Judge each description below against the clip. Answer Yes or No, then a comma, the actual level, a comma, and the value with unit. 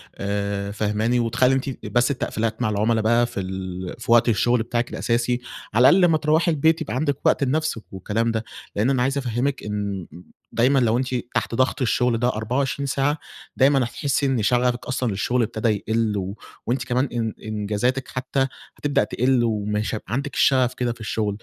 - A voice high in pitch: No, low, 120 Hz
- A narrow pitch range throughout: No, average, 3.4 semitones